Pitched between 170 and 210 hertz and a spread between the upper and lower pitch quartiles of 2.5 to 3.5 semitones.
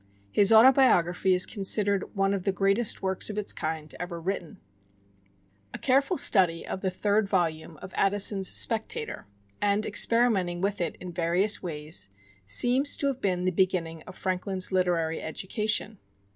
Yes: high, 190 Hz; average, 3.1 semitones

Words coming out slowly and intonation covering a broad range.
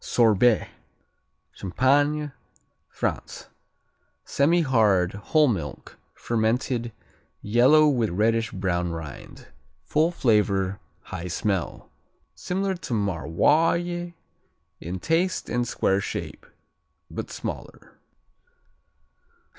Yes: slow, 80 wpm; wide, 7.6 semitones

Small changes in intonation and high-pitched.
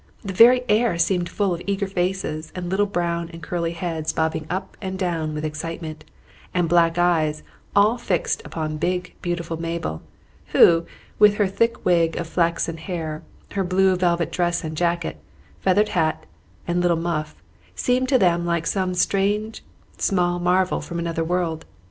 No: narrow, 2.3 semitones; medium, 175 Hz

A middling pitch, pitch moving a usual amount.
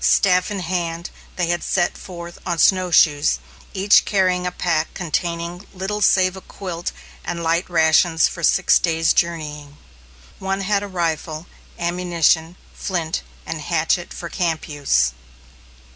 No: medium, 170 Hz; narrow, 2.2 semitones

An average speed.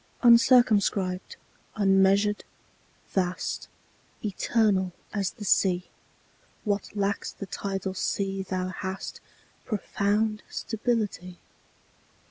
No: slow, 80 wpm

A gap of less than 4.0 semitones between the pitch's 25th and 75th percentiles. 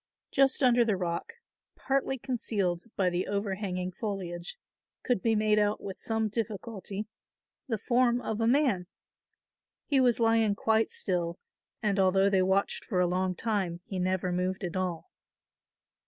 Yes: average, 3.6 semitones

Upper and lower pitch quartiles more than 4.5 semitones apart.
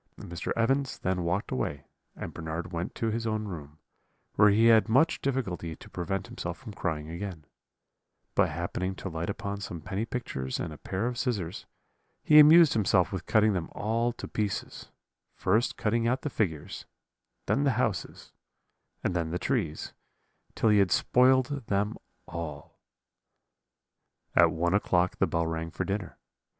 Yes: average, 5.2 semitones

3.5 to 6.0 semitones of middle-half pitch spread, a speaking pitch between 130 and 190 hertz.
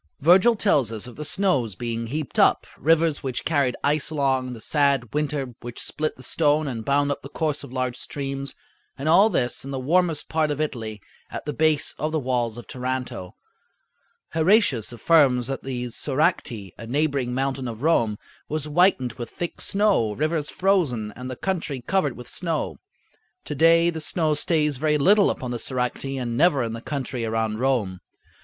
Yes: average, 4.2 semitones; medium, 140 Hz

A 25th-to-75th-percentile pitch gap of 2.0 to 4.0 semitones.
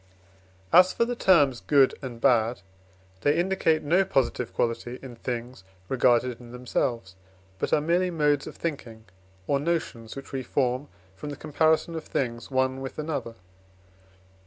No: average, 4.6 semitones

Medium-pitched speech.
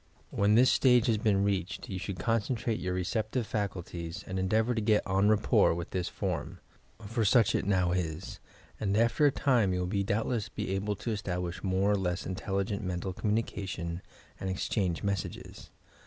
No: low, 100 Hz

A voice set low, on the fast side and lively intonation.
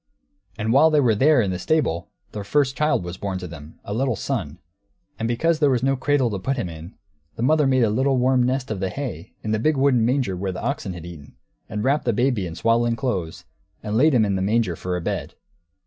Yes: low, 115 Hz; fast, 240 wpm; wide, 6.1 semitones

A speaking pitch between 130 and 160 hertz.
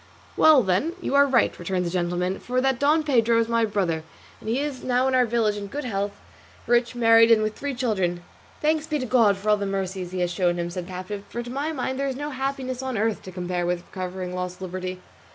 No: high, 220 Hz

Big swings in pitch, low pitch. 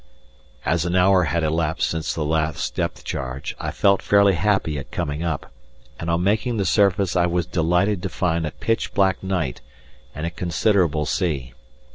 No: average, 3.5 semitones; very low, 85 Hz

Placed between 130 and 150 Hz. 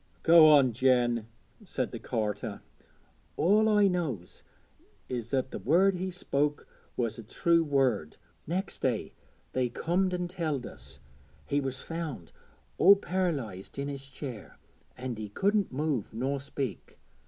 Yes: medium, 140 Hz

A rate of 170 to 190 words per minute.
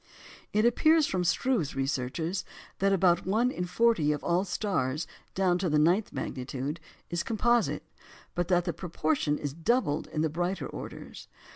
No: average, 155 wpm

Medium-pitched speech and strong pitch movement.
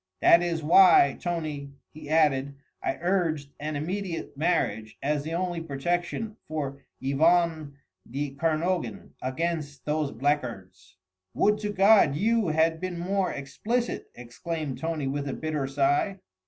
No: medium, 155 Hz; average, 3.7 semitones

